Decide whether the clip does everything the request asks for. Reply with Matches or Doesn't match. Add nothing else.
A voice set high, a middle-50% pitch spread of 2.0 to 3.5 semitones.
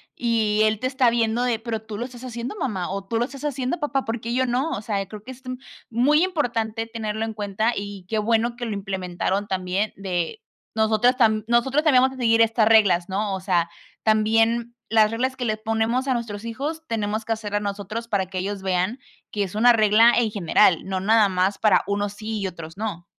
Matches